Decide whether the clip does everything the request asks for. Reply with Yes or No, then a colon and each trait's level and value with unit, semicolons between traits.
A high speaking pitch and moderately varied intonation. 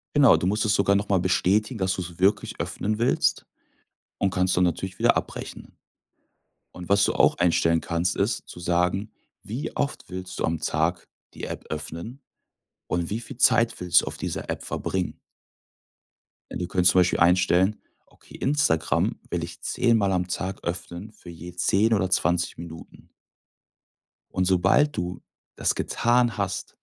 No: very low, 90 Hz; average, 3.2 semitones